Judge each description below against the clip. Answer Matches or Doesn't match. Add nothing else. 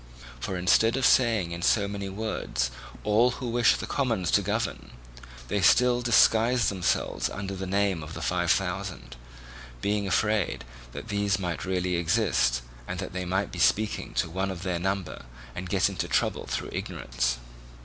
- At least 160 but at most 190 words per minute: Matches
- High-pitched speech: Doesn't match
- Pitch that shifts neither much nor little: Matches